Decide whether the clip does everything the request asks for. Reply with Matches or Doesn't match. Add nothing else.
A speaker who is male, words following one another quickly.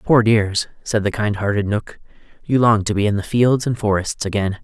Matches